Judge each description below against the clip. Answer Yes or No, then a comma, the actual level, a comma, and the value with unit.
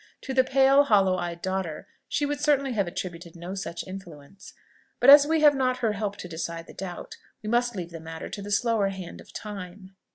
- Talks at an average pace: No, fast, 215 wpm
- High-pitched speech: Yes, high, 195 Hz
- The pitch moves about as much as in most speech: No, wide, 6.4 semitones